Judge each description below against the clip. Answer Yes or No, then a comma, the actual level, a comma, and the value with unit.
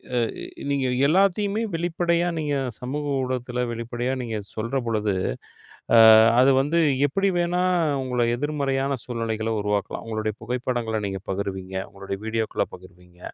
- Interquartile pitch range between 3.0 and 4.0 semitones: No, average, 4.9 semitones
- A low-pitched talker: Yes, low, 125 Hz